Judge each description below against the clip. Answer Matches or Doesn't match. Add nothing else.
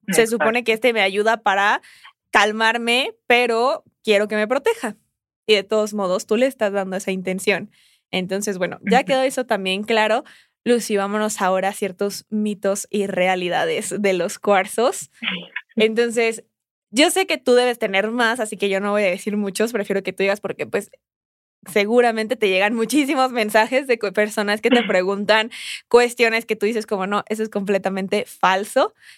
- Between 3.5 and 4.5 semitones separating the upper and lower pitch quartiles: Doesn't match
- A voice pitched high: Matches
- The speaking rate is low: Doesn't match